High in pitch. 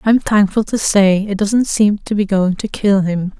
Yes: high, 205 Hz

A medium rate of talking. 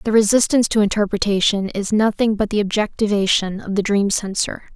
Yes: average, 165 wpm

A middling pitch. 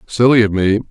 No: low, 110 Hz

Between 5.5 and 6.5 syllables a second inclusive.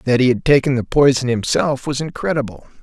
Yes: 5.6 syllables/s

